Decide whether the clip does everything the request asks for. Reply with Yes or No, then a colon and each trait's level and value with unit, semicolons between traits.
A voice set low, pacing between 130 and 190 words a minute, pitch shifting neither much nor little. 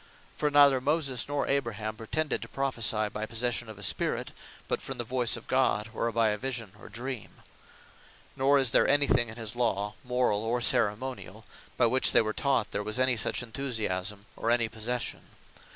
Yes: low, 120 Hz; average, 185 wpm; average, 3.3 semitones